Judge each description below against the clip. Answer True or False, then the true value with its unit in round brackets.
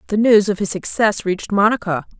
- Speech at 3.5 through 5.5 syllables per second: False (5.8 syllables/s)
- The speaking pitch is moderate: False (200 Hz)